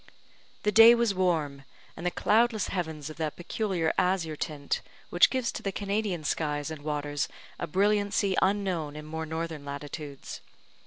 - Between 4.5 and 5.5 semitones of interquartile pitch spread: Yes, average, 4.8 semitones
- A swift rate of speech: No, average, 155 wpm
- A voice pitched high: No, medium, 165 Hz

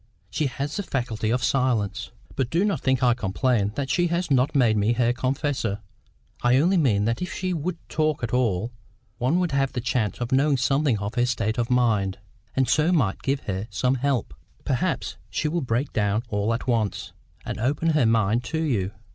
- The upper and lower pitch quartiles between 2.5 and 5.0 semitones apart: Yes, average, 4.3 semitones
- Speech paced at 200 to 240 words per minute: Yes, fast, 205 wpm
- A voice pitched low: Yes, low, 125 Hz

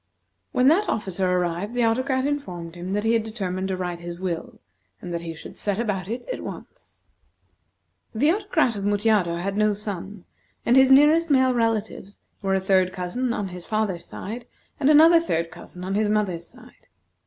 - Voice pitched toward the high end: Yes, high, 205 Hz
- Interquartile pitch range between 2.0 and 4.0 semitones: No, average, 5.1 semitones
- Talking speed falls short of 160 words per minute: No, average, 185 wpm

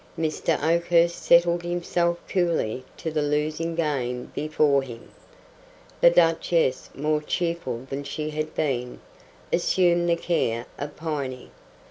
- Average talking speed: No, slow, 120 wpm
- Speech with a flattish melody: No, average, 3.5 semitones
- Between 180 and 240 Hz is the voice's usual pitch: No, medium, 155 Hz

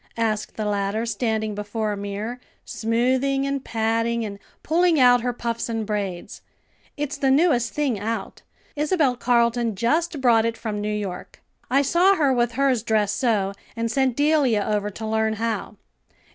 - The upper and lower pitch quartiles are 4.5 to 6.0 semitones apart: No, average, 3.7 semitones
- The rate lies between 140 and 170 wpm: Yes, average, 160 wpm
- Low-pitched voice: No, high, 230 Hz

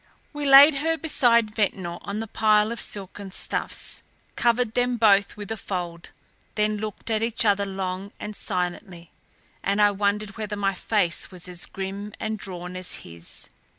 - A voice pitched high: Yes, high, 205 Hz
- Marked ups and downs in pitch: No, average, 2.7 semitones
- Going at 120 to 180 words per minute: Yes, average, 165 wpm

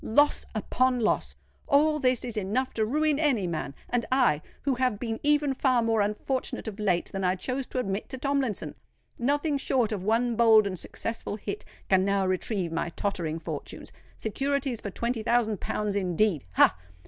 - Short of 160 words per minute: No, average, 170 wpm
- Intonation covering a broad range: No, average, 4.6 semitones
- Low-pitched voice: No, high, 225 Hz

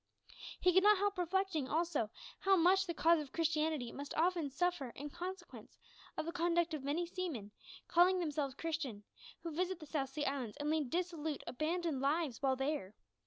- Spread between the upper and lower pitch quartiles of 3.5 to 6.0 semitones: Yes, average, 3.9 semitones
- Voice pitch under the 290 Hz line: No, very high, 320 Hz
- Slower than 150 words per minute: No, average, 175 wpm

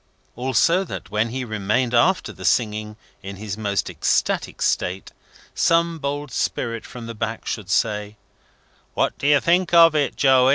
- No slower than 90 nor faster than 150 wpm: No, average, 160 wpm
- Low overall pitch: Yes, low, 120 Hz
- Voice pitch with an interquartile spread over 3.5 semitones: Yes, wide, 5.5 semitones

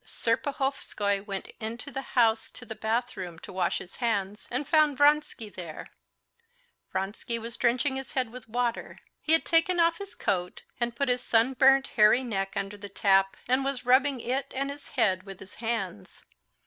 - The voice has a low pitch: No, high, 235 Hz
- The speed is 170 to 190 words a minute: Yes, average, 175 wpm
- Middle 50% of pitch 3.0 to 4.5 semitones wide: No, average, 5.0 semitones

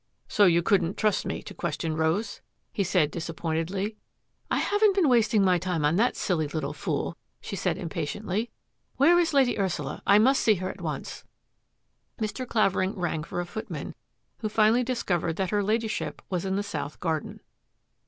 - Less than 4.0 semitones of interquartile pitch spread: No, average, 4.7 semitones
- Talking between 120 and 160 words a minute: No, average, 185 wpm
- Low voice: No, high, 190 Hz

